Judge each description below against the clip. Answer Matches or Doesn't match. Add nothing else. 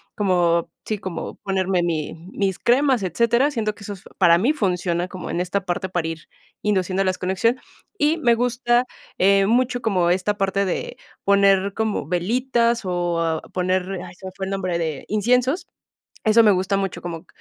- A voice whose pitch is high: Matches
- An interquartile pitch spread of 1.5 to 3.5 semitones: Doesn't match